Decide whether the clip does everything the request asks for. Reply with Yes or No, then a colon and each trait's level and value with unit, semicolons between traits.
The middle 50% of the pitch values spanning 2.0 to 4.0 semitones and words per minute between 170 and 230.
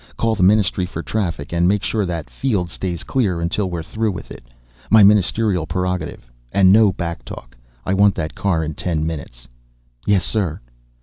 Yes: average, 3.5 semitones; average, 180 wpm